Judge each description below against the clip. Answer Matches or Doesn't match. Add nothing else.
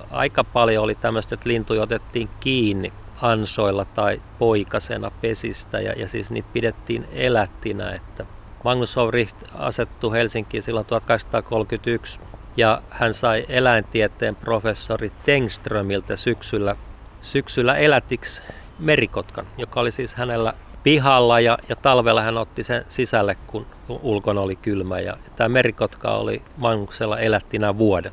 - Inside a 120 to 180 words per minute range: Matches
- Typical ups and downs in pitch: Doesn't match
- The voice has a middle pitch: Doesn't match